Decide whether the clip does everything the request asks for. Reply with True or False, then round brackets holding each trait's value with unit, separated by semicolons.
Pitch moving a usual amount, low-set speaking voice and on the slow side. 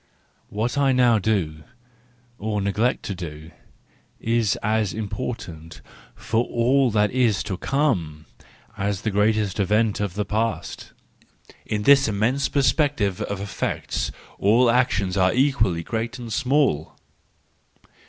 True (3.8 semitones; 110 Hz; 125 wpm)